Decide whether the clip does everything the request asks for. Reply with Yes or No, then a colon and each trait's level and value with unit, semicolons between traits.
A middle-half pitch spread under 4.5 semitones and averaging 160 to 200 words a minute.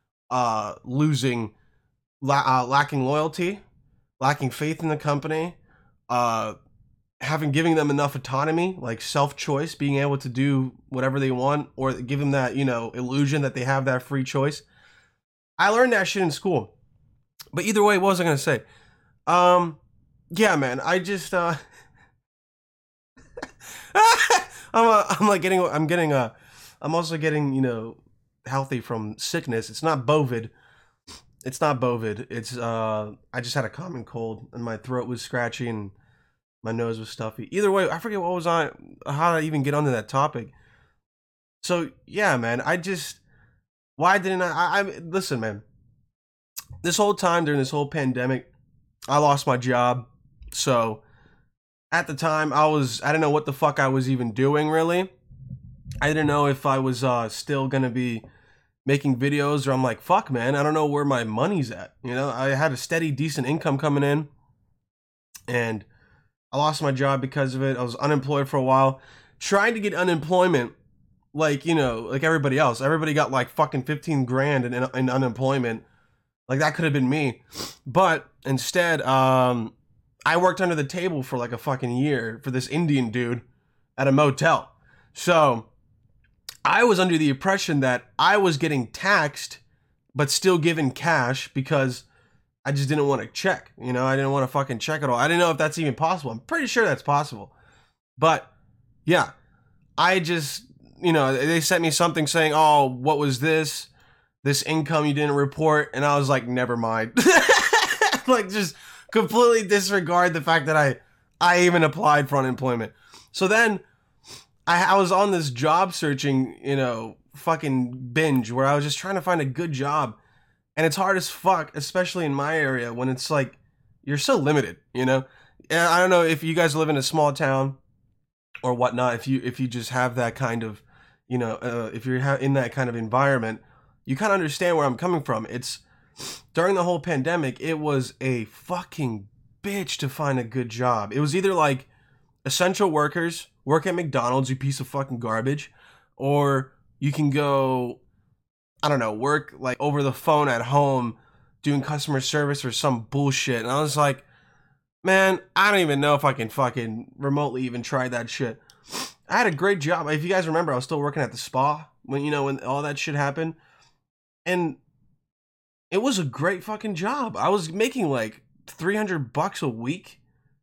Yes: average, 4.0 semitones; average, 180 wpm